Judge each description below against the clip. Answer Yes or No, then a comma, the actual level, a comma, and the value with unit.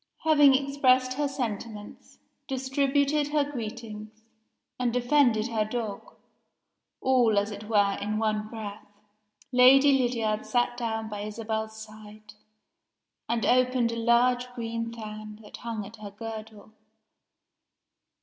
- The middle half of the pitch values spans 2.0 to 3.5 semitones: Yes, average, 3.0 semitones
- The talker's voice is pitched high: Yes, high, 230 Hz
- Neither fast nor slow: No, slow, 120 wpm